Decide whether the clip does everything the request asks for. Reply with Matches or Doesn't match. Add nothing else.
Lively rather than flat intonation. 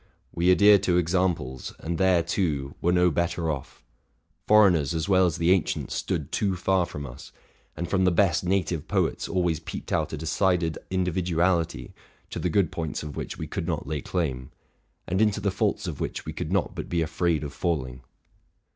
Doesn't match